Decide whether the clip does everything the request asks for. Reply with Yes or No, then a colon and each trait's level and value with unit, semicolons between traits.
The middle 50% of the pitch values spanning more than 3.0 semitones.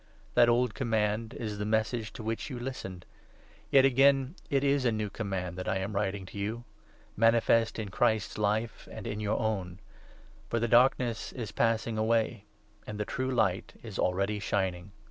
No: average, 2.7 semitones